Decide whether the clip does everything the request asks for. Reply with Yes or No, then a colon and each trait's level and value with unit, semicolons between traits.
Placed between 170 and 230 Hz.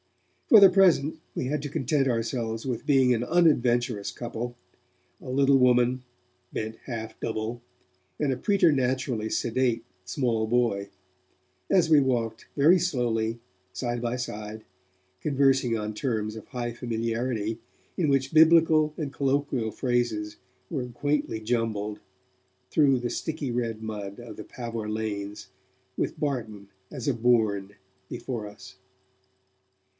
No: low, 120 Hz